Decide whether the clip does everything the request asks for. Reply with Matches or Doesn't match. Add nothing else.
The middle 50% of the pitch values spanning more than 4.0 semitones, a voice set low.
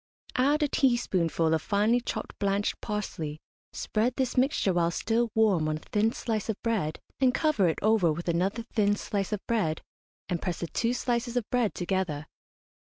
Doesn't match